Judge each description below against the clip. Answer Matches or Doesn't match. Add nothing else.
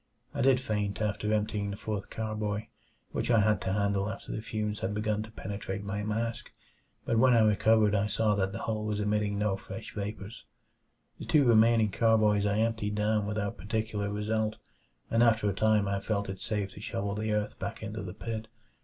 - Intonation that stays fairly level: Matches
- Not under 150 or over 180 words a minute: Doesn't match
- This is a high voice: Doesn't match